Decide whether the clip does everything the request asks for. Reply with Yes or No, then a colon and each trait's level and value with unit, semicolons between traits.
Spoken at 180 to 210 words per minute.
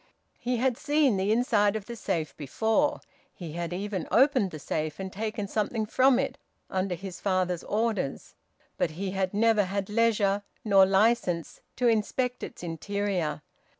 No: average, 155 wpm